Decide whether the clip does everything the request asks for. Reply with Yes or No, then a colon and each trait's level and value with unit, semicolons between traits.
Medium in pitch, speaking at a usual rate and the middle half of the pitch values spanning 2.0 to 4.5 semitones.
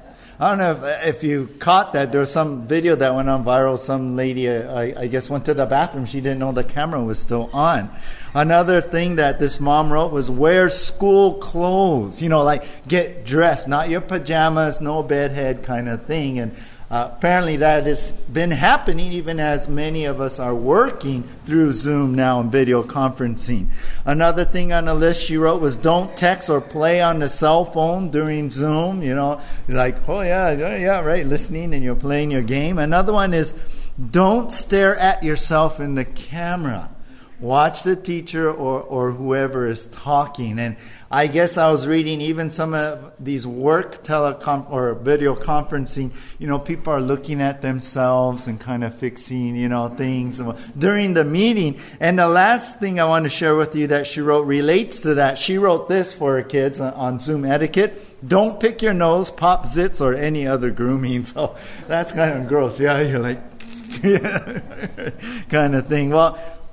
Yes: medium, 150 Hz; average, 185 wpm; average, 4.0 semitones